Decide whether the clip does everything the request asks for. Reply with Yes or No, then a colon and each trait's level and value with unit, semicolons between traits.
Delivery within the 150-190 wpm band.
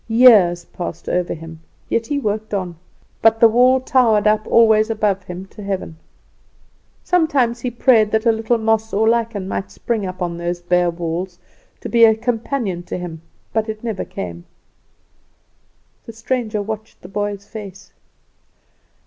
Yes: average, 155 wpm